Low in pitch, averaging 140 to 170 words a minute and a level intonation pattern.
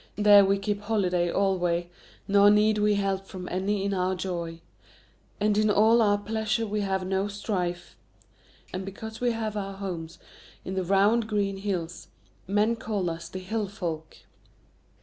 No: high, 200 Hz; average, 160 wpm; narrow, 2.3 semitones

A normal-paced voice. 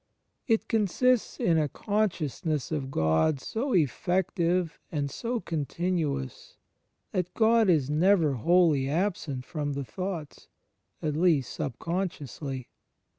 No: slow, 110 wpm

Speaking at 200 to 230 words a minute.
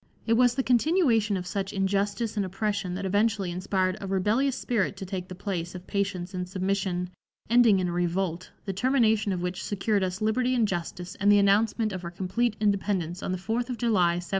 Yes: fast, 205 wpm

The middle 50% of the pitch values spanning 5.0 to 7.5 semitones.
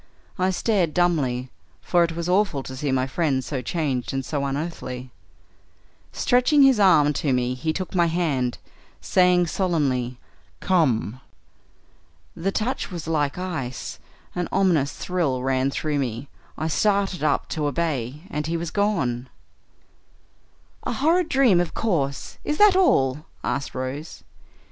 Yes: wide, 5.5 semitones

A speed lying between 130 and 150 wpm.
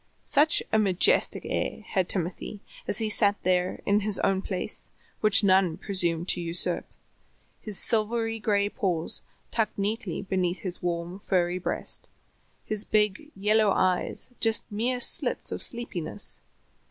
Yes: average, 140 wpm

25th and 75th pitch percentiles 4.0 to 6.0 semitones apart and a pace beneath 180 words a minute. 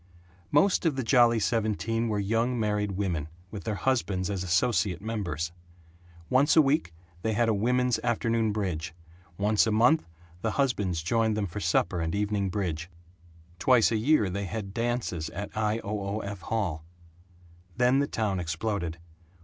No: average, 3.6 semitones; average, 160 wpm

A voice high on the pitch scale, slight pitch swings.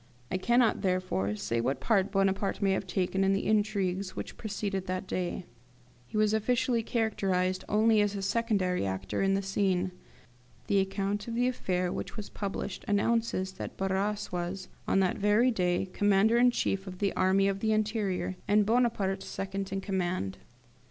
Yes: high, 195 Hz; narrow, 2.3 semitones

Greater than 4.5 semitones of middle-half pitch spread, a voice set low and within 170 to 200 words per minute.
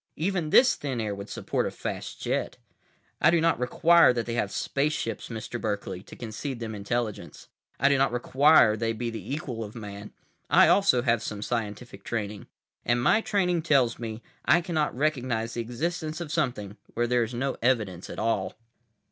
Yes: average, 5.1 semitones; low, 120 Hz; average, 180 wpm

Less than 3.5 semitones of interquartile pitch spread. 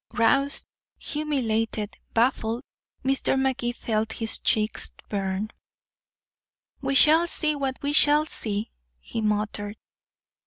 No: average, 4.4 semitones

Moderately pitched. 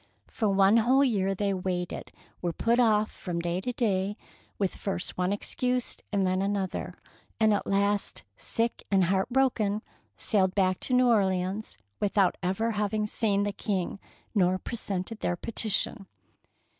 No: high, 200 Hz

